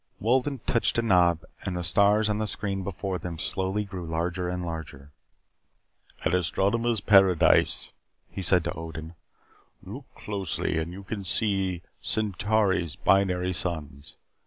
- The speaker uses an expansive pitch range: No, average, 3.1 semitones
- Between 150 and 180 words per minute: No, slow, 135 wpm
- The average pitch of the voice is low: Yes, very low, 95 Hz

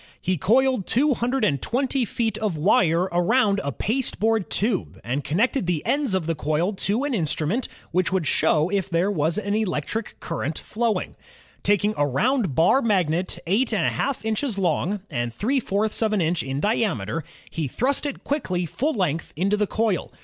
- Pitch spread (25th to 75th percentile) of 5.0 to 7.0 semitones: Yes, wide, 5.6 semitones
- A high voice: Yes, high, 200 Hz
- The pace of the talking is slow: No, average, 170 wpm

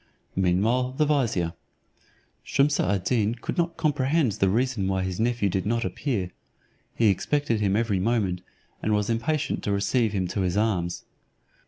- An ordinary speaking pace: Yes, average, 160 wpm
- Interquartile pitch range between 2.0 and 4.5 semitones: No, average, 5.0 semitones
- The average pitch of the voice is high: No, low, 110 Hz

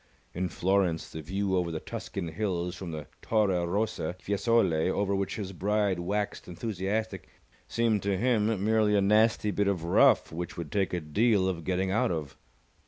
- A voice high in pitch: No, very low, 95 Hz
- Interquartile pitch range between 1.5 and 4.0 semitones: Yes, average, 3.2 semitones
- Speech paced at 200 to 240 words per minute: No, average, 170 wpm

